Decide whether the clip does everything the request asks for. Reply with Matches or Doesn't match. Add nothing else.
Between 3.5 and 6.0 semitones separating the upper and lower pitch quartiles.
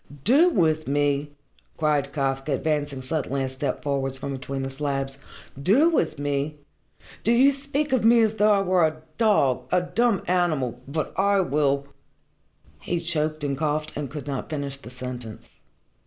Matches